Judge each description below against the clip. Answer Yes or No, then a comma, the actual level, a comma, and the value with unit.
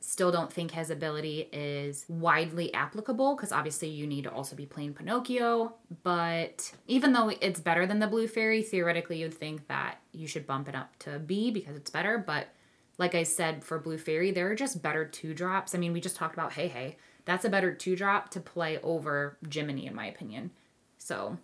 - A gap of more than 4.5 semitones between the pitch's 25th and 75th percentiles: No, average, 3.8 semitones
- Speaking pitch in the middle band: Yes, medium, 165 Hz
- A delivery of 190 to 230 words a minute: Yes, fast, 205 wpm